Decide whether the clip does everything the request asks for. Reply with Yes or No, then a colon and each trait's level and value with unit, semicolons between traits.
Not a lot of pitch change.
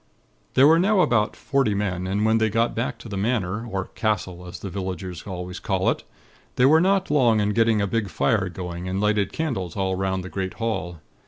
No: average, 3.7 semitones